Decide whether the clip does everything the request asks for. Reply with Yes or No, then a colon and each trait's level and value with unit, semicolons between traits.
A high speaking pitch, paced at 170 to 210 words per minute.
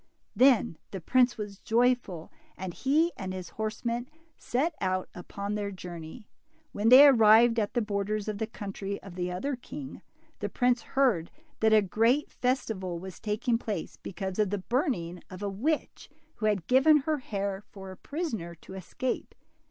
Yes: high, 215 Hz; average, 175 wpm